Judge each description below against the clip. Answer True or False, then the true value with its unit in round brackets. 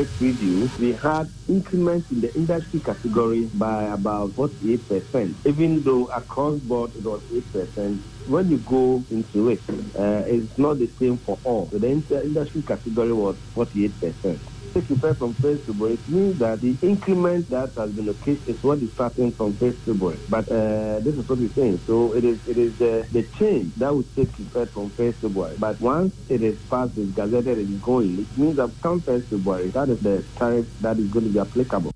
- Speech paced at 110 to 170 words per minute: False (205 wpm)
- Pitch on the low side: True (120 Hz)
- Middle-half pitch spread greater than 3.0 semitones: True (3.9 semitones)